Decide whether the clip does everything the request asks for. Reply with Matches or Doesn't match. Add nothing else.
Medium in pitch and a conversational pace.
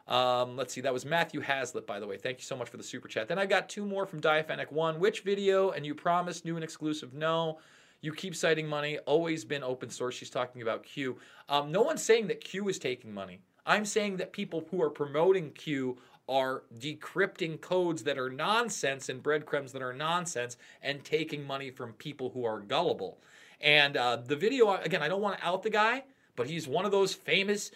Doesn't match